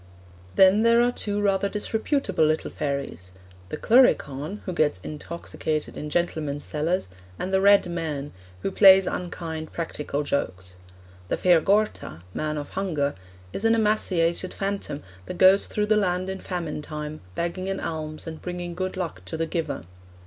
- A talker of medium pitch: Yes, medium, 175 Hz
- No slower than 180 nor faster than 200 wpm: No, average, 155 wpm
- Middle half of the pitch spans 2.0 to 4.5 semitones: Yes, average, 4.2 semitones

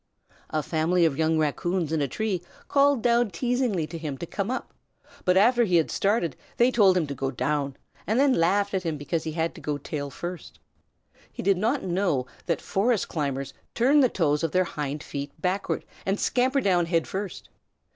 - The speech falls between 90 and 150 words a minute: No, average, 195 wpm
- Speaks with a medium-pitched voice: Yes, medium, 175 Hz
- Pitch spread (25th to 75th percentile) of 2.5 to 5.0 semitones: No, wide, 5.4 semitones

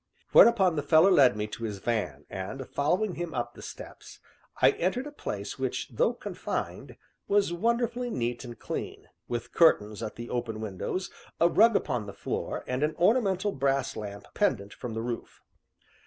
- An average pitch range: No, wide, 8.9 semitones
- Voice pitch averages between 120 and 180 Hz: Yes, low, 135 Hz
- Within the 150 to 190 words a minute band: Yes, average, 170 wpm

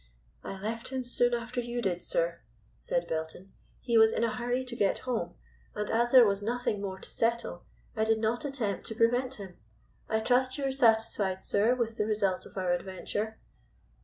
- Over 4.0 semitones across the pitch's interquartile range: No, average, 3.2 semitones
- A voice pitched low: No, high, 225 Hz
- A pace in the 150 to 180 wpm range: No, average, 190 wpm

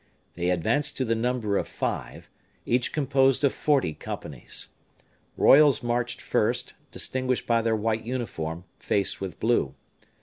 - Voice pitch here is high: No, low, 120 Hz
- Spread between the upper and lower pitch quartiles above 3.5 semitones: Yes, average, 4.5 semitones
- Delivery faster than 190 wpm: No, slow, 135 wpm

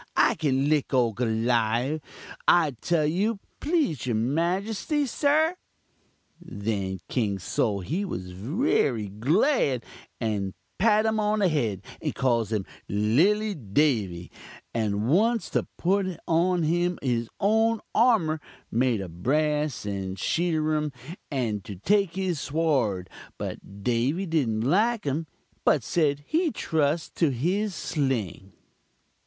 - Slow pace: Yes, slow, 125 wpm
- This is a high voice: No, medium, 150 Hz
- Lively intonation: Yes, wide, 8.7 semitones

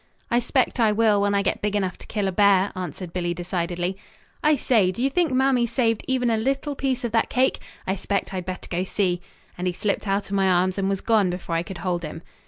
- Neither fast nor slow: No, fast, 250 wpm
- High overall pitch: Yes, high, 200 Hz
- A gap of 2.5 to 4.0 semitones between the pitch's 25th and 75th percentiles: No, average, 4.5 semitones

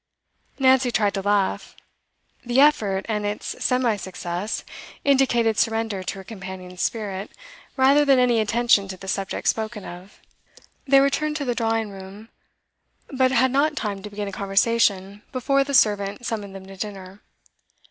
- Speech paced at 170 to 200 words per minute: No, average, 155 wpm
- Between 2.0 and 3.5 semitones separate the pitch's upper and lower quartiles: No, average, 4.3 semitones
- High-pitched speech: Yes, high, 215 Hz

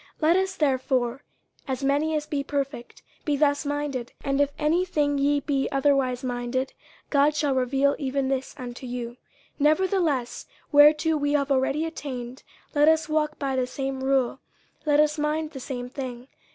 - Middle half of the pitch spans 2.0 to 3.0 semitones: Yes, narrow, 2.4 semitones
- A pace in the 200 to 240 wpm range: No, average, 175 wpm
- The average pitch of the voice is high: Yes, very high, 280 Hz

